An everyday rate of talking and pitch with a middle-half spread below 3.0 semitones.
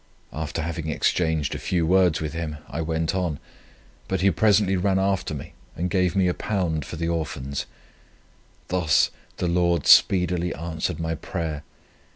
Yes: average, 155 wpm; narrow, 2.4 semitones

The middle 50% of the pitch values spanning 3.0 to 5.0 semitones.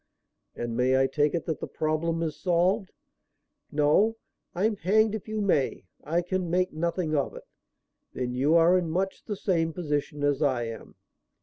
Yes: average, 4.0 semitones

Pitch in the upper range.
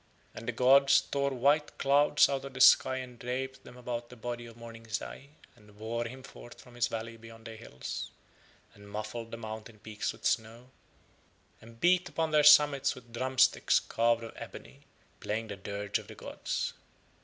No: low, 120 Hz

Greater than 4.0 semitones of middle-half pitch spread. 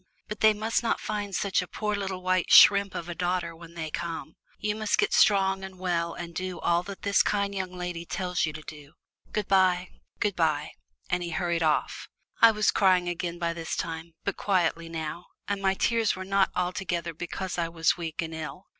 No: average, 2.8 semitones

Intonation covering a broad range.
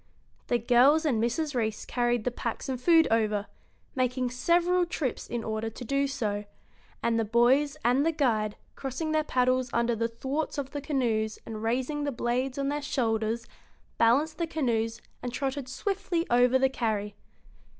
No: average, 3.8 semitones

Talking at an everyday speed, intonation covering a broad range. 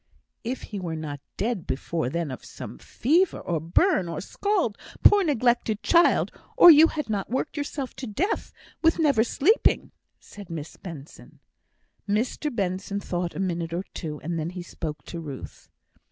Yes: average, 165 wpm; wide, 9.0 semitones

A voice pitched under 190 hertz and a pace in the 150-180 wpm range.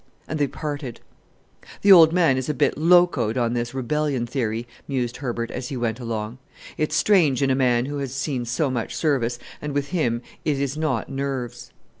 No: low, 135 Hz; average, 190 wpm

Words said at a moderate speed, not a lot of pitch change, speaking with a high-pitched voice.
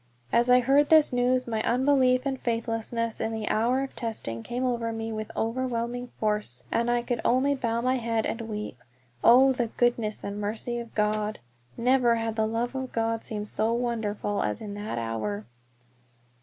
Yes: average, 180 wpm; narrow, 2.3 semitones; high, 230 Hz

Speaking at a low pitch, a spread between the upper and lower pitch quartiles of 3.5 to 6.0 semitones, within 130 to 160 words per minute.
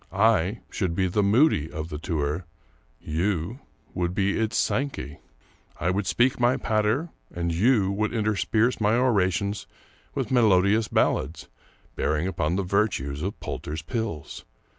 Yes: low, 100 Hz; average, 4.7 semitones; average, 140 wpm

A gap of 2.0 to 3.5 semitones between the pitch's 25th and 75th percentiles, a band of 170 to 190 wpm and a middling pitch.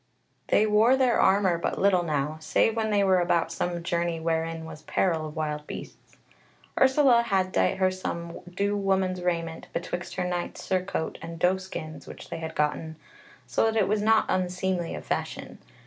Yes: average, 3.1 semitones; average, 180 wpm; medium, 180 Hz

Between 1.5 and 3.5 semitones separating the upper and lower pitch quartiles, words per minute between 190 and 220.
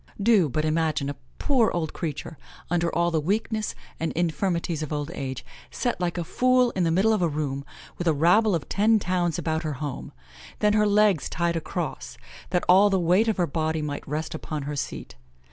No: average, 4.3 semitones; average, 200 wpm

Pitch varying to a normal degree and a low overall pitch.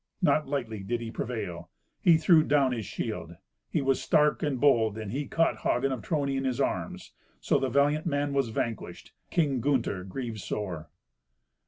Yes: average, 4.6 semitones; low, 130 Hz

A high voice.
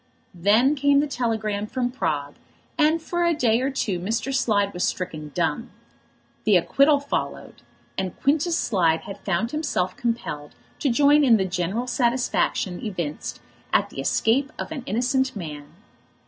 Yes: high, 230 Hz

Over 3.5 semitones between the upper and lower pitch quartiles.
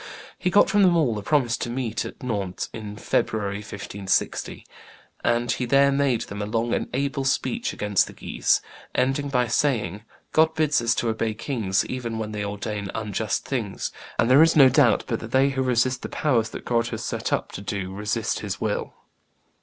Yes: average, 4.5 semitones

